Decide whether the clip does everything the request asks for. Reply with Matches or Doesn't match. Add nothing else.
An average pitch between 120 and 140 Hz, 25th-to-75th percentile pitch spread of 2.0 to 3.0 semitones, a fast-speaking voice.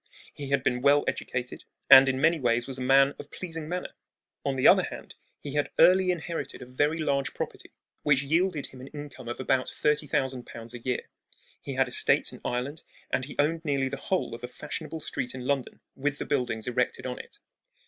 Matches